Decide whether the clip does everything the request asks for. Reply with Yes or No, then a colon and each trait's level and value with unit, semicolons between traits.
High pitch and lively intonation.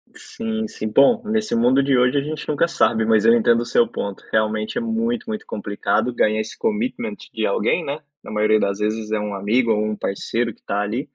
No: low, 115 Hz; wide, 7.7 semitones